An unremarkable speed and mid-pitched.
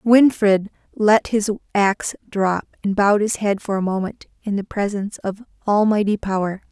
No: average, 160 wpm; high, 205 Hz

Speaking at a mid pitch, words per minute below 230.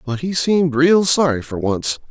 Yes: medium, 150 Hz; average, 200 wpm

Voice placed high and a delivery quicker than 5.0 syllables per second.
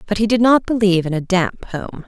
Yes: high, 200 Hz; 5.7 syllables/s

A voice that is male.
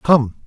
Yes: male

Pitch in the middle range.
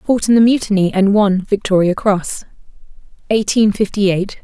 No: high, 200 Hz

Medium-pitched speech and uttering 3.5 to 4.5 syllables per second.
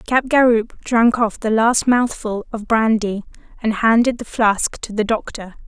No: high, 225 Hz; 4.4 syllables/s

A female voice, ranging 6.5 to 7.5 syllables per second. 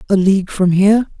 No: male; 6.7 syllables/s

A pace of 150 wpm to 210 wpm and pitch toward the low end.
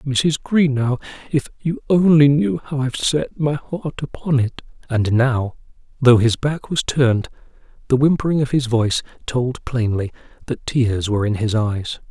Yes: average, 165 wpm; low, 130 Hz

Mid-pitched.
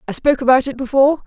No: very high, 265 Hz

